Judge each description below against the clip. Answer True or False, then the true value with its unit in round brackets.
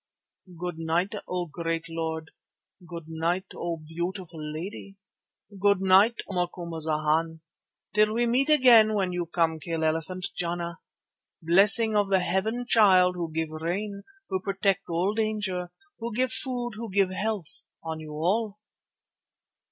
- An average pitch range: True (4.1 semitones)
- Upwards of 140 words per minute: False (135 wpm)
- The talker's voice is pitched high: False (180 Hz)